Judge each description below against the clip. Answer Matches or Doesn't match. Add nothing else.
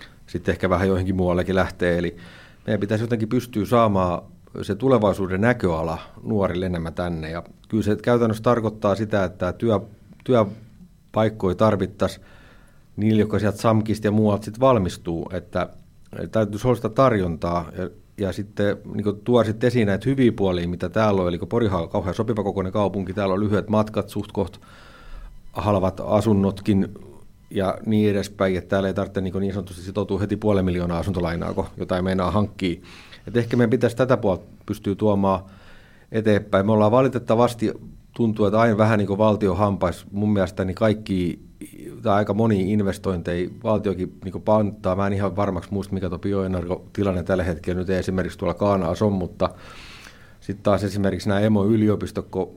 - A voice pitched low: Matches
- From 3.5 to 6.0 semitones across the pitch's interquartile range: Doesn't match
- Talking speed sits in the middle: Doesn't match